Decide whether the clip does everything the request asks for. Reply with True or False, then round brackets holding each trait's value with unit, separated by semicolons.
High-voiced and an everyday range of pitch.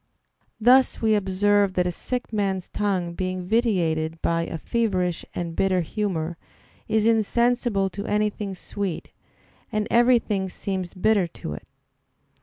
True (195 Hz; 3.3 semitones)